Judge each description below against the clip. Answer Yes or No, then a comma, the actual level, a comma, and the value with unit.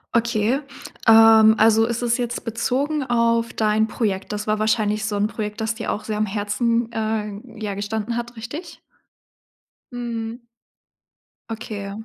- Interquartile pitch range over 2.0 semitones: No, narrow, 1.7 semitones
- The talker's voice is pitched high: Yes, high, 225 Hz